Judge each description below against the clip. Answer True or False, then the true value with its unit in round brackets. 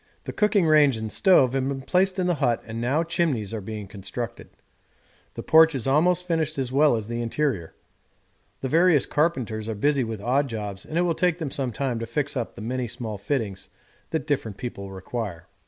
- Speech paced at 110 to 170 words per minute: False (205 wpm)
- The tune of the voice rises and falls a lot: True (5.7 semitones)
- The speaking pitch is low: True (130 Hz)